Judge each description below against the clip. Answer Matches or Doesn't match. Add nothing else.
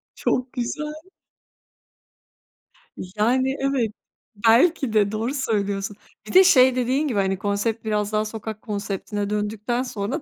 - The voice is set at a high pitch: Matches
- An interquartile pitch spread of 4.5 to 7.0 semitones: Doesn't match